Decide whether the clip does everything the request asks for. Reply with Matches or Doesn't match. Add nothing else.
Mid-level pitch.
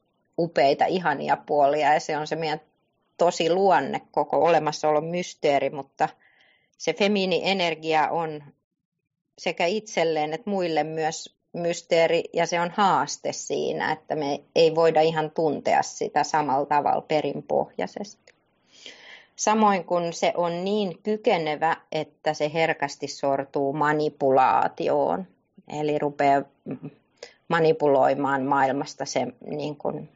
Matches